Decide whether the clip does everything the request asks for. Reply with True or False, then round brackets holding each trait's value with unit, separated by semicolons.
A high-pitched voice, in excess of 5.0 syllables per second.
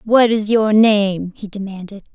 False (205 Hz; 4.2 syllables/s)